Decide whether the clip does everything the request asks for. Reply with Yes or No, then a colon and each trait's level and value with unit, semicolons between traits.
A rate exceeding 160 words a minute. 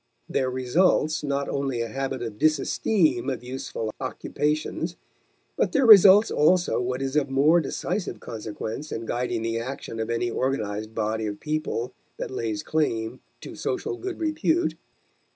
No: average, 150 wpm